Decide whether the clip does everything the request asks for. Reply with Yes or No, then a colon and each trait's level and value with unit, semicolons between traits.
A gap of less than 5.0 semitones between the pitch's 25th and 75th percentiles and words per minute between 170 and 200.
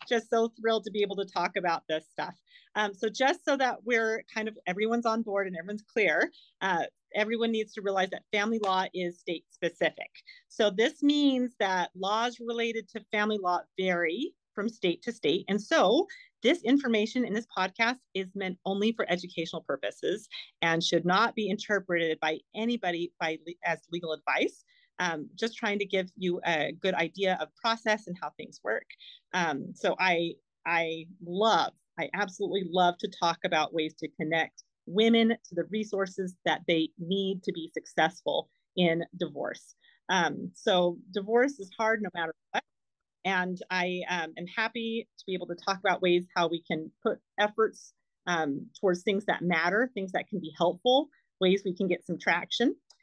Yes: average, 4.3 semitones; average, 180 wpm